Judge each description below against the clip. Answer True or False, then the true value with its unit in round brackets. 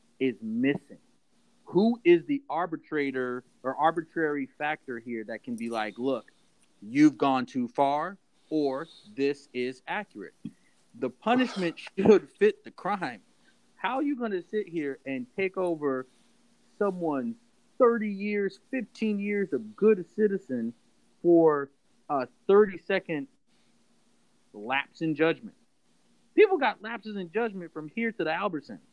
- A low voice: False (185 Hz)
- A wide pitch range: True (7.9 semitones)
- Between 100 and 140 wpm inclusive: True (135 wpm)